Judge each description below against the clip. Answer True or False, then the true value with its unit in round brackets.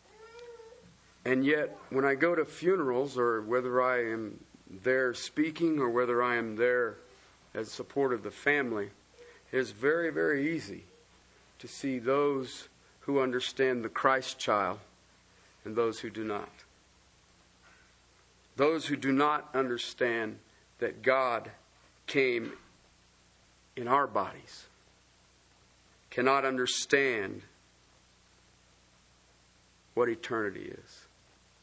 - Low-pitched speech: True (125 Hz)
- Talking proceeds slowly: True (110 wpm)